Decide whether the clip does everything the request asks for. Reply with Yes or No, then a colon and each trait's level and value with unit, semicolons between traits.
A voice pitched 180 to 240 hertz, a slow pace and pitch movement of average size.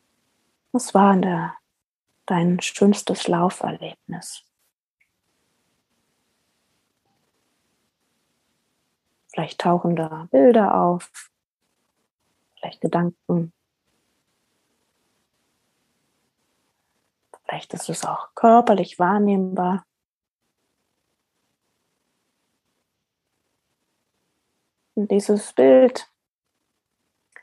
Yes: medium, 185 Hz; slow, 50 wpm; average, 3.0 semitones